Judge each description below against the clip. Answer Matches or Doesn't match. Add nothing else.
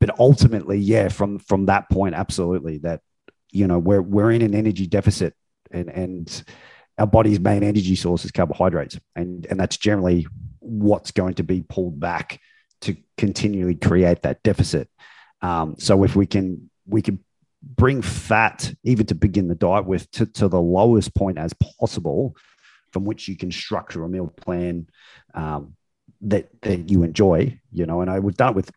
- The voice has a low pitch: Matches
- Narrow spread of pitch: Doesn't match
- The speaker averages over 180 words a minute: Doesn't match